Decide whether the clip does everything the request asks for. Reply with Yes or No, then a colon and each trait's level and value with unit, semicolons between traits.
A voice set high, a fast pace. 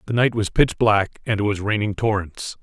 No: low, 105 Hz; fast, 230 wpm